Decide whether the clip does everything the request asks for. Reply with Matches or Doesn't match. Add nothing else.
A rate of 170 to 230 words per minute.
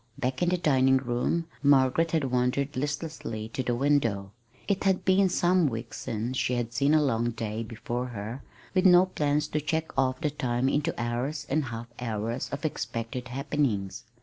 Matches